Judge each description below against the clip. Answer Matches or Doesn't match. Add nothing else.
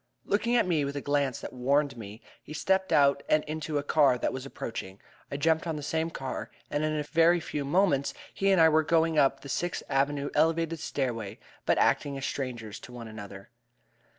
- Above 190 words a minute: Matches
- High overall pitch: Doesn't match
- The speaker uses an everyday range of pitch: Matches